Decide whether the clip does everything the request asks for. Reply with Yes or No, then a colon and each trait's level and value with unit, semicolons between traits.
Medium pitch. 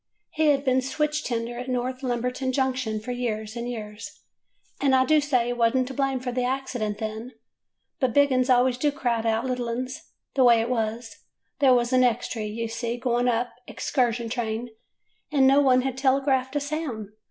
No: very high, 250 Hz